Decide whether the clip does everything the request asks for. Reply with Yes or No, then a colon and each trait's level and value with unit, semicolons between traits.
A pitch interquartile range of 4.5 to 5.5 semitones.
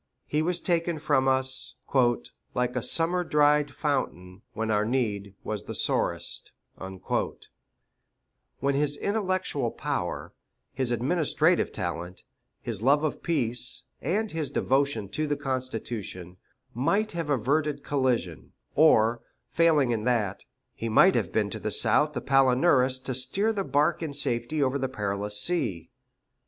Yes: average, 5.0 semitones